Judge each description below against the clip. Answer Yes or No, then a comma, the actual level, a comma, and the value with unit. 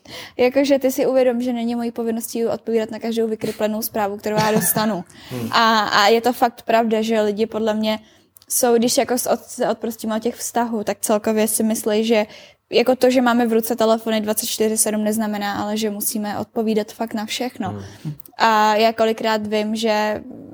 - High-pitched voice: Yes, high, 225 Hz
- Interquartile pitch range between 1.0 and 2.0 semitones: Yes, narrow, 1.6 semitones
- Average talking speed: No, fast, 175 wpm